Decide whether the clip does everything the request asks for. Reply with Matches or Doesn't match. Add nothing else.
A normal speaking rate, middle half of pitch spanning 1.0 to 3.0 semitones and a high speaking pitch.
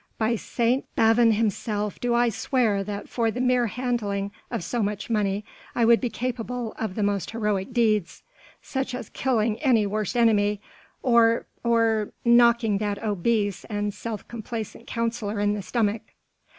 Matches